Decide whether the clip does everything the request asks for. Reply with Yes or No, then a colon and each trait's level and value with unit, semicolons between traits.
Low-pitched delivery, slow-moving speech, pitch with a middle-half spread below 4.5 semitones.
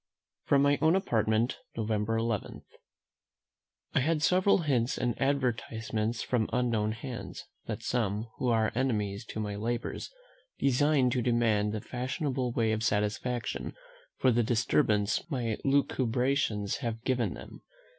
Yes: low, 120 Hz; slow, 130 wpm; average, 3.1 semitones